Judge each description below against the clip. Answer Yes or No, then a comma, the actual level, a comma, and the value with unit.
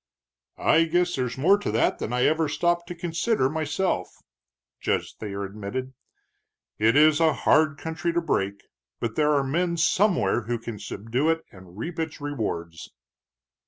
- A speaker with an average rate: Yes, average, 160 wpm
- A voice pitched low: No, medium, 150 Hz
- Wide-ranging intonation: Yes, wide, 6.6 semitones